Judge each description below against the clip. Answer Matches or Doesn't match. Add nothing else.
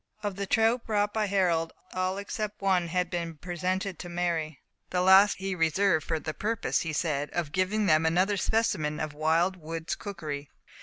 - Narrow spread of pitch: Doesn't match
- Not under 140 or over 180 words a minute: Doesn't match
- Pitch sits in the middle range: Matches